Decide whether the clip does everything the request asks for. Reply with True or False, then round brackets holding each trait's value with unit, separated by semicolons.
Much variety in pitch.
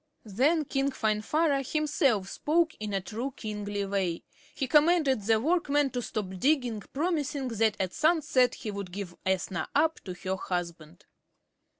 True (6.8 semitones)